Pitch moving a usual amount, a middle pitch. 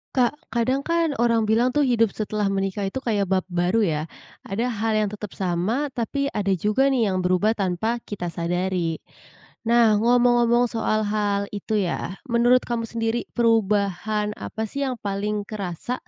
No: average, 3.2 semitones; high, 215 Hz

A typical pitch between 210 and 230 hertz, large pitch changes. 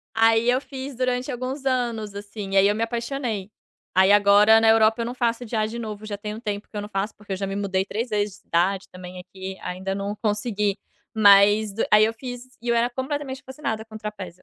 No: high, 215 Hz; average, 2.9 semitones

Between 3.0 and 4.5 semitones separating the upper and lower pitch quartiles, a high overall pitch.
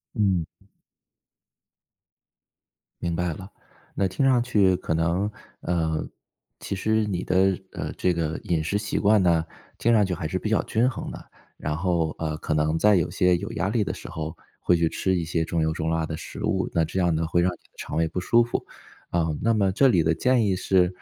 No: average, 3.8 semitones; very low, 90 Hz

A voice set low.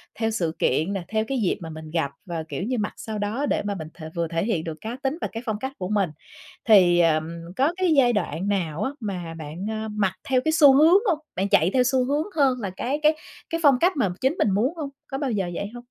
No: high, 215 Hz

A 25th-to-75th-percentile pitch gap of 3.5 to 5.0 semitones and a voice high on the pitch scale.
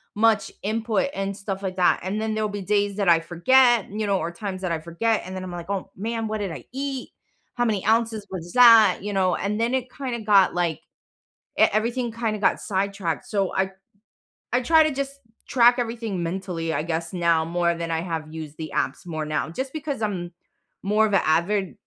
Yes: average, 4.6 semitones; high, 200 Hz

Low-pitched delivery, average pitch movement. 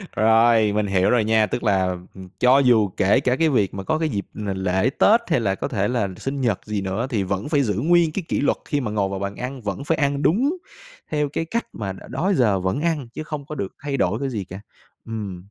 No: low, 115 Hz; wide, 6.2 semitones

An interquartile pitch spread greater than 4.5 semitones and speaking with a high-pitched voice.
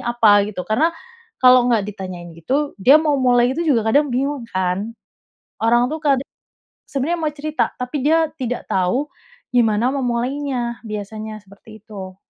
Yes: average, 4.9 semitones; high, 245 Hz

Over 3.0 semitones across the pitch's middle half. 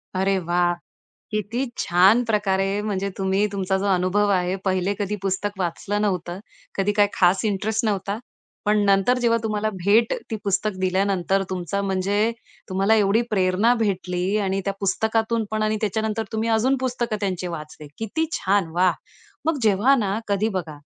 No: narrow, 2.5 semitones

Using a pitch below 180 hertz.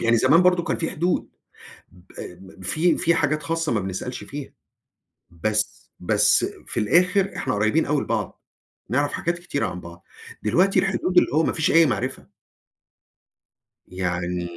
Yes: medium, 140 Hz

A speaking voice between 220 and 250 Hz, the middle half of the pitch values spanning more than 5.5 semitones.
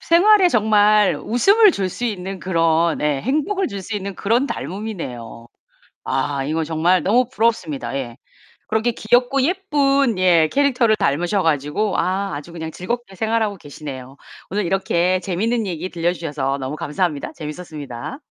No: high, 190 Hz; wide, 6.5 semitones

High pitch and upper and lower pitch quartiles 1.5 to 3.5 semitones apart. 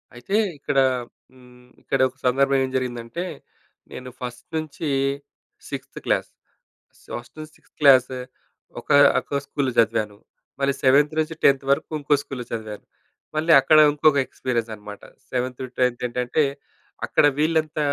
No: low, 130 Hz; average, 3.0 semitones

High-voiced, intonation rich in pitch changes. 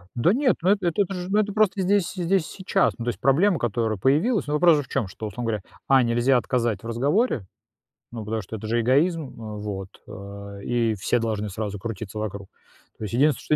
No: low, 120 Hz; wide, 8.1 semitones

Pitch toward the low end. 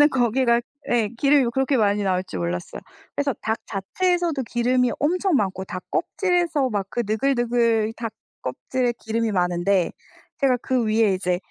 No: high, 235 Hz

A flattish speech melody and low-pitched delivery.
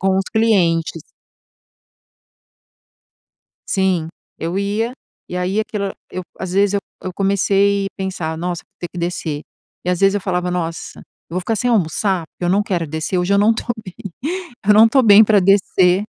No: narrow, 2.3 semitones; high, 190 Hz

